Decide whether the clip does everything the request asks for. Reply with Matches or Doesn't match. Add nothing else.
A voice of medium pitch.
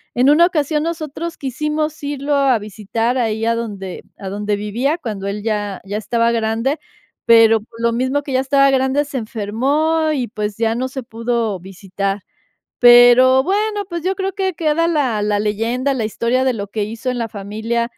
Doesn't match